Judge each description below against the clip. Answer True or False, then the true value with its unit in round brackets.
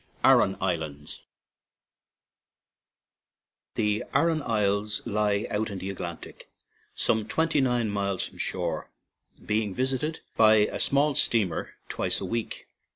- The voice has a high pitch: False (105 Hz)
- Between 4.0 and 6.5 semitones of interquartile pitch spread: False (3.5 semitones)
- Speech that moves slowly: True (115 wpm)